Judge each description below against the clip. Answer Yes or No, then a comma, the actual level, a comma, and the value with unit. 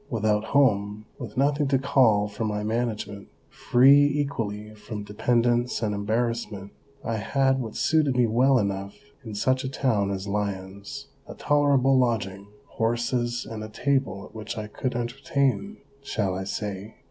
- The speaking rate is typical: Yes, average, 155 wpm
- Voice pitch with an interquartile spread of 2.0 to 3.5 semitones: No, average, 4.1 semitones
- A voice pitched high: No, low, 115 Hz